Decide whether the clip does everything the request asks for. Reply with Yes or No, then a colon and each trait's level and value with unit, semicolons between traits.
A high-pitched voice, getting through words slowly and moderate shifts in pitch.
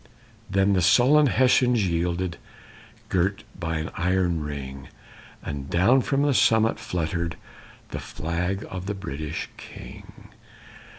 No: very low, 90 Hz; slow, 120 wpm; average, 4.1 semitones